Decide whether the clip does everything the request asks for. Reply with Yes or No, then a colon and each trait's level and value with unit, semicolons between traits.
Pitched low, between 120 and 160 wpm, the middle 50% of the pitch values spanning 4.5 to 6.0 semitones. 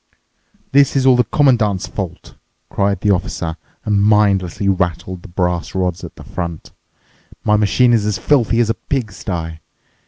No: low, 100 Hz; average, 150 wpm; average, 4.1 semitones